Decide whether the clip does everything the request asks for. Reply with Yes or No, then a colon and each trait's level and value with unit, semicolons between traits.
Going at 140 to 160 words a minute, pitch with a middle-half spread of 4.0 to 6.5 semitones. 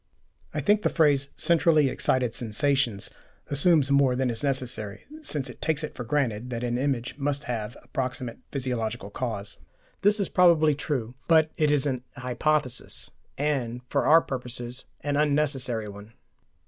No: average, 155 wpm; average, 3.6 semitones